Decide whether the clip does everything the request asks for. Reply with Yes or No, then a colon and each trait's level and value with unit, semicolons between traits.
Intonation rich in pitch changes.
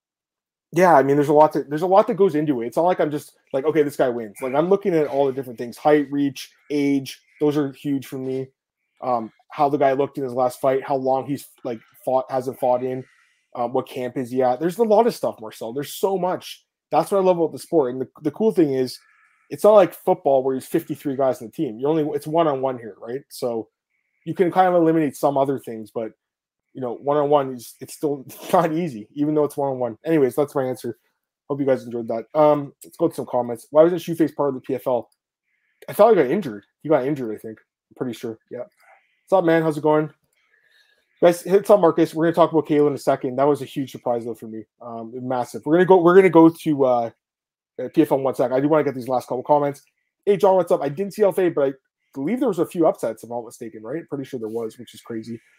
No: average, 3.9 semitones